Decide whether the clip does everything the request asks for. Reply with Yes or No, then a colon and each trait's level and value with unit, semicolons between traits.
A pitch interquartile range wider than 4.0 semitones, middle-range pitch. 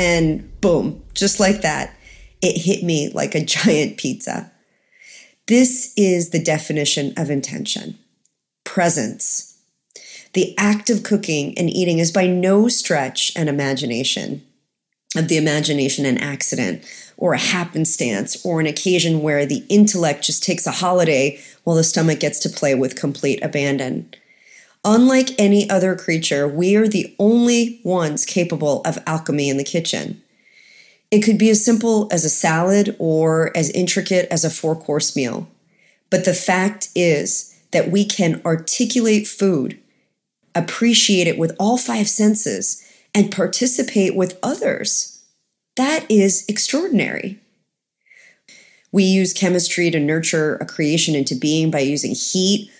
Yes: average, 4.6 semitones; medium, 180 Hz